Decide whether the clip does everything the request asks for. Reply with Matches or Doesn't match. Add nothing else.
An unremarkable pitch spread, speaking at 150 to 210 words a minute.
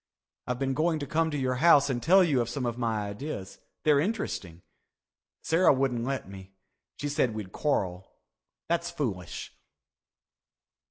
Doesn't match